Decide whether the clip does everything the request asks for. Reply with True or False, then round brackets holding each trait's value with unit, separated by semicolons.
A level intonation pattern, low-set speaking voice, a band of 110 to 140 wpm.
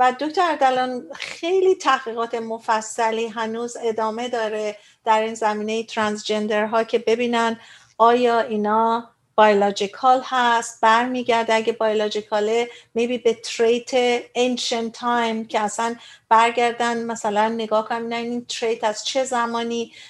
False (1.4 semitones; 230 Hz; 115 wpm)